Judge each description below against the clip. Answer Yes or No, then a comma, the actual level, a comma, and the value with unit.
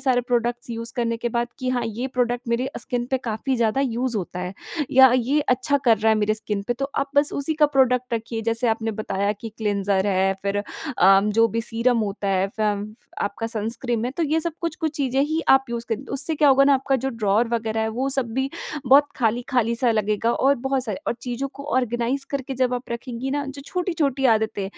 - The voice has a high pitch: Yes, high, 240 Hz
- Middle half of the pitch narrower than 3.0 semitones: No, average, 3.3 semitones